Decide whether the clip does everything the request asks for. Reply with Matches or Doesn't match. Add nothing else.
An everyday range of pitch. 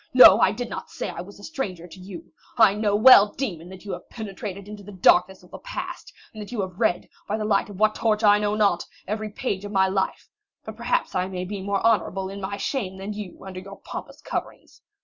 Doesn't match